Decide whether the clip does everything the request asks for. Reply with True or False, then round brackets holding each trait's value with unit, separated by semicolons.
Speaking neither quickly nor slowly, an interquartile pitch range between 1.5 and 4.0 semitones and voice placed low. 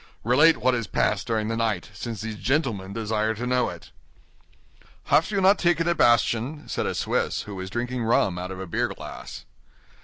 True (190 wpm; 3.3 semitones; 115 Hz)